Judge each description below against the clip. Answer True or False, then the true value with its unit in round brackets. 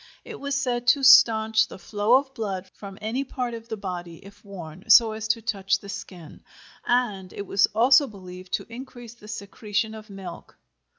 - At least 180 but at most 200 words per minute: True (185 wpm)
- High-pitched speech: True (220 Hz)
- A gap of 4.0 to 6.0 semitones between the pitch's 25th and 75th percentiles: False (3.6 semitones)